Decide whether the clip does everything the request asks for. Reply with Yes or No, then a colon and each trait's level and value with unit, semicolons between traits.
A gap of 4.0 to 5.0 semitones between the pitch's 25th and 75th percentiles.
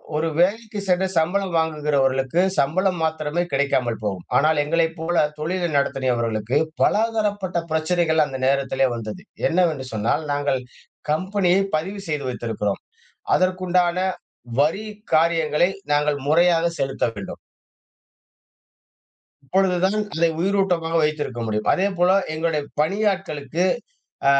Yes: average, 4.5 semitones